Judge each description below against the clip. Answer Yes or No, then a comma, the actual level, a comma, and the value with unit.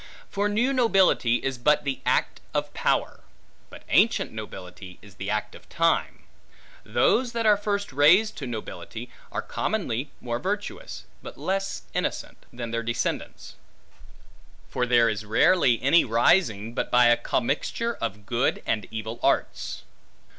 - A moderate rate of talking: Yes, average, 145 wpm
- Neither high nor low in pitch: No, low, 125 Hz